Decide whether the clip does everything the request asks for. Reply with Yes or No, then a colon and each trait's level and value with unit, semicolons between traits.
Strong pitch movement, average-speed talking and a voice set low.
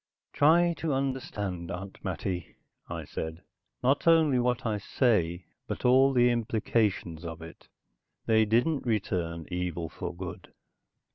No: wide, 6.5 semitones; slow, 130 wpm; low, 105 Hz